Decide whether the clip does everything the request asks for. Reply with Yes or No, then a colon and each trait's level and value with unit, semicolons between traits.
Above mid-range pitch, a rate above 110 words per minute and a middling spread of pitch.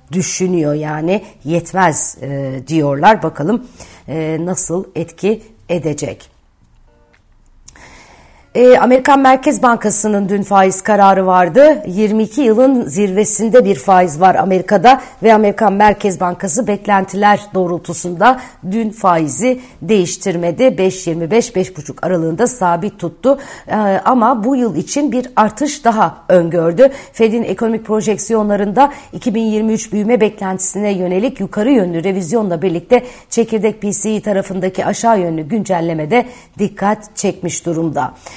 No: high, 200 Hz; average, 105 wpm; average, 4.3 semitones